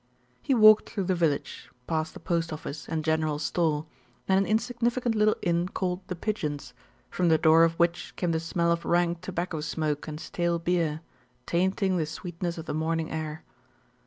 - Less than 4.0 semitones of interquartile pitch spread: Yes, narrow, 2.5 semitones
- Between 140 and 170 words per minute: No, average, 180 wpm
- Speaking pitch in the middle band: Yes, medium, 170 Hz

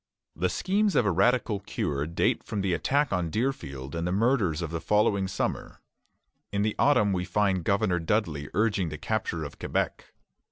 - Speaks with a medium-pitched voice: No, very low, 95 Hz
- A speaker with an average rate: Yes, average, 175 wpm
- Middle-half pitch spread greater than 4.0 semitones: Yes, average, 4.5 semitones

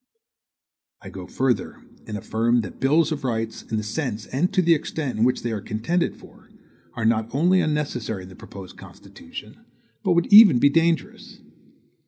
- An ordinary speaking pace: Yes, average, 175 wpm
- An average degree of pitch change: No, wide, 6.6 semitones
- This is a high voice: No, low, 125 Hz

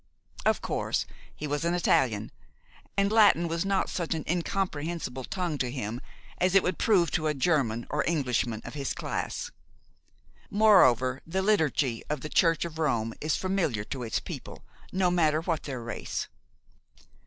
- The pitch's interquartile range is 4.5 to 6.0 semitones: Yes, wide, 5.6 semitones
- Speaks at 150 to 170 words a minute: Yes, average, 160 wpm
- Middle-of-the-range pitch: Yes, medium, 155 Hz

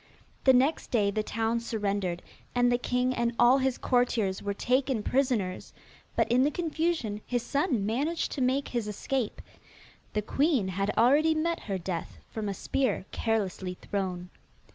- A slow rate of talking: No, average, 160 wpm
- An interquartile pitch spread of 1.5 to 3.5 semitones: No, average, 4.7 semitones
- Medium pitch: No, high, 235 Hz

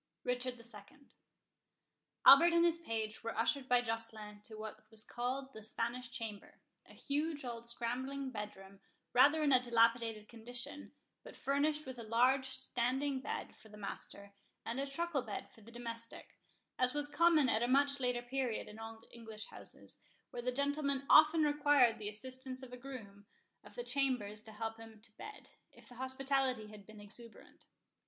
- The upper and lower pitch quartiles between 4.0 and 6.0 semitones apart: No, average, 3.5 semitones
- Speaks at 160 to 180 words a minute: Yes, average, 170 wpm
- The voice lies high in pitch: Yes, high, 245 Hz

